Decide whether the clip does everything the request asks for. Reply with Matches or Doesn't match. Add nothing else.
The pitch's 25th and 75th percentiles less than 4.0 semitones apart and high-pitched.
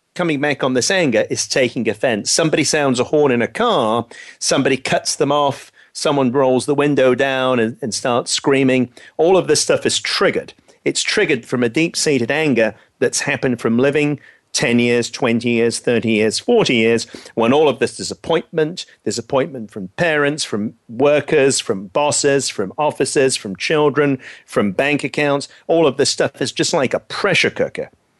Doesn't match